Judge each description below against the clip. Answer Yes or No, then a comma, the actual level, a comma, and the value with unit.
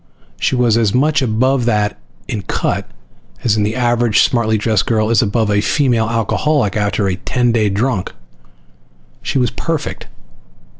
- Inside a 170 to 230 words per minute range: No, average, 150 wpm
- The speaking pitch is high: No, low, 115 Hz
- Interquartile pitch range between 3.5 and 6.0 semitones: No, average, 2.9 semitones